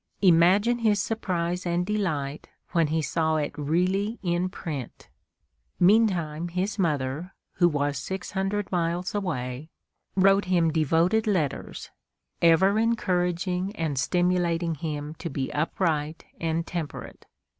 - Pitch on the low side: No, medium, 175 Hz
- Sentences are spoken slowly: Yes, slow, 120 wpm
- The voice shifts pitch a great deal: No, average, 3.3 semitones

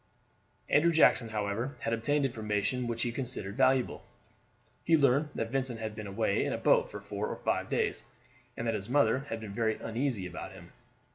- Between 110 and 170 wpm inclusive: No, average, 180 wpm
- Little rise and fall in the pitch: No, average, 3.8 semitones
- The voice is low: Yes, low, 115 Hz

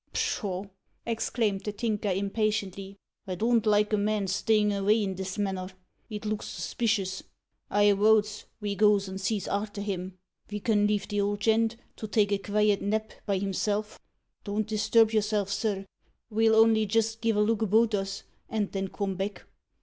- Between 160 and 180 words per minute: Yes, average, 165 wpm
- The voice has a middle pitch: No, high, 210 Hz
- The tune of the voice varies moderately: No, narrow, 1.7 semitones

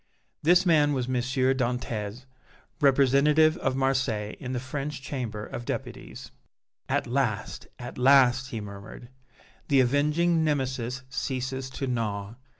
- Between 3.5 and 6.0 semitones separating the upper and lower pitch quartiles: No, narrow, 2.4 semitones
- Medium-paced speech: No, slow, 125 wpm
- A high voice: No, low, 130 Hz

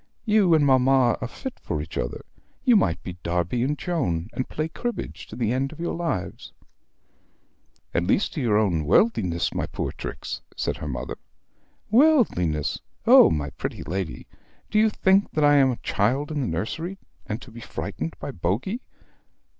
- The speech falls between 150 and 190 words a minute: Yes, average, 180 wpm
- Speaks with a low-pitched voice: Yes, low, 125 Hz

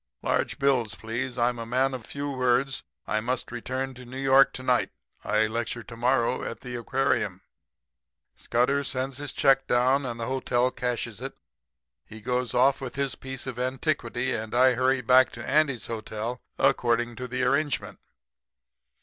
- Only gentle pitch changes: Yes, narrow, 1.9 semitones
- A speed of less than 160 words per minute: No, average, 165 wpm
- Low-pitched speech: Yes, low, 125 Hz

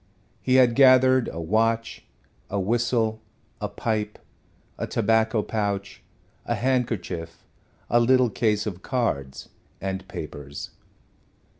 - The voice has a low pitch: Yes, low, 110 Hz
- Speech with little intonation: No, average, 3.3 semitones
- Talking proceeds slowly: Yes, slow, 110 wpm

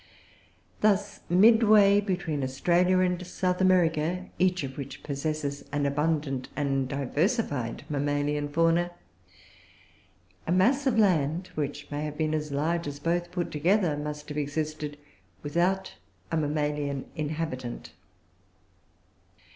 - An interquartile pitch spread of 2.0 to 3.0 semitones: No, average, 3.8 semitones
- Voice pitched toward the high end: No, medium, 155 Hz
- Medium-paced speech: No, slow, 115 wpm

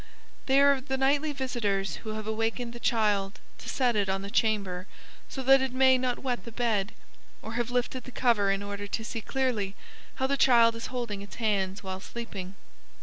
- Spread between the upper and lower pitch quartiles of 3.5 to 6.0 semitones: Yes, average, 4.0 semitones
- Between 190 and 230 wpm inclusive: Yes, average, 200 wpm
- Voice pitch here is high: Yes, high, 230 Hz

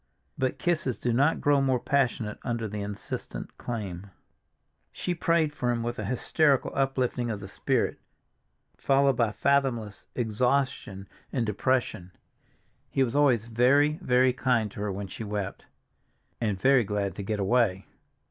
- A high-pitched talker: No, low, 120 Hz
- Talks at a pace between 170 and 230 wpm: No, average, 145 wpm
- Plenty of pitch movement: No, average, 4.4 semitones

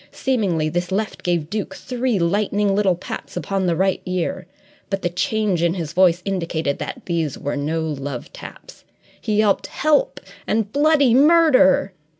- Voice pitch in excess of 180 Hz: Yes, high, 190 Hz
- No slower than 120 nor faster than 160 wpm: Yes, average, 155 wpm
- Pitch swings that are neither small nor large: Yes, average, 4.2 semitones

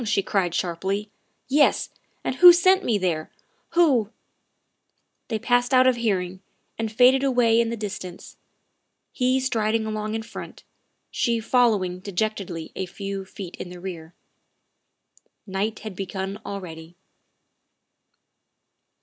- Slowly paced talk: Yes, slow, 130 wpm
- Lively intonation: No, average, 4.1 semitones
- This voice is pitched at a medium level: No, high, 215 Hz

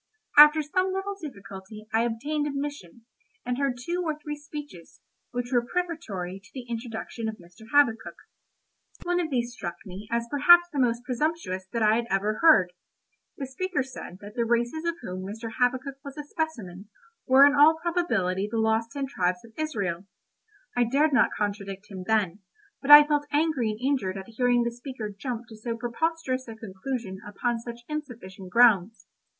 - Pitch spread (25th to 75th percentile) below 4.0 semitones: No, wide, 5.5 semitones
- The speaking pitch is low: No, high, 240 Hz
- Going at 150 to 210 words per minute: Yes, average, 175 wpm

